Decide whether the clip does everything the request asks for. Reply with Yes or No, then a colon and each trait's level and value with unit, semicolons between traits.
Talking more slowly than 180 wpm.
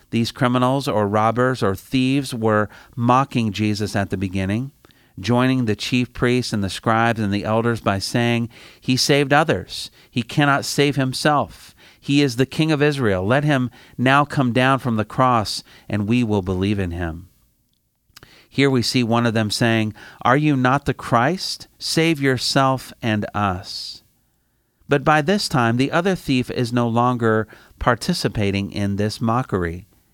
Yes: average, 160 wpm